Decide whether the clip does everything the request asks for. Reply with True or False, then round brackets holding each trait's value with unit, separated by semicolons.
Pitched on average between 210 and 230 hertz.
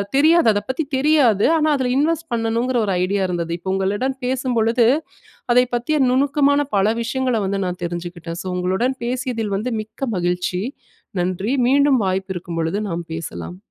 True (225 Hz)